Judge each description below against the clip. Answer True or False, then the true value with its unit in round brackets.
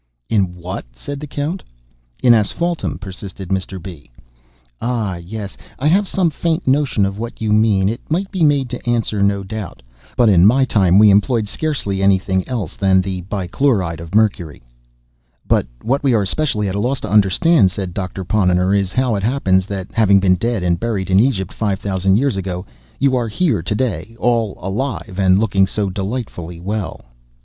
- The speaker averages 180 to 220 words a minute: True (185 wpm)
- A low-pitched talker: True (100 Hz)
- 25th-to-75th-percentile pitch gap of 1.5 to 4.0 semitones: False (4.4 semitones)